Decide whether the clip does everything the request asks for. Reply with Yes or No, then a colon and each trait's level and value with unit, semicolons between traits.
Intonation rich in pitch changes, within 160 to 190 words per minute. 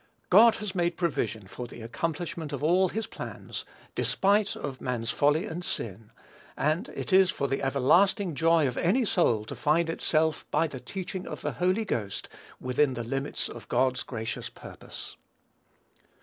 Yes: wide, 6.1 semitones; average, 165 wpm